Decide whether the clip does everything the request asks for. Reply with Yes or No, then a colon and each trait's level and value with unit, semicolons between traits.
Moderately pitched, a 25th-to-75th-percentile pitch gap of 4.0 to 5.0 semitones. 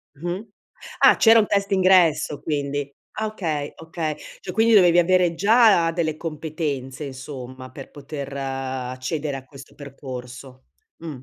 Yes: medium, 150 Hz; average, 4.6 semitones